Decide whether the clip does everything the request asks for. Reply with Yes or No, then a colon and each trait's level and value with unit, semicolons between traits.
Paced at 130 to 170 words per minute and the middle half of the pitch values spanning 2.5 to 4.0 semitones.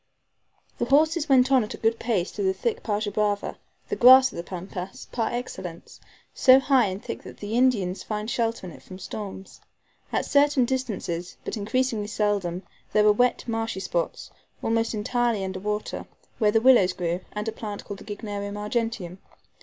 No: average, 180 wpm; average, 3.7 semitones